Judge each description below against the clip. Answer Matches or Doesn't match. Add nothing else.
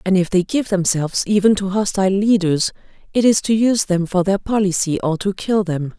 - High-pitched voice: Matches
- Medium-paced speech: Doesn't match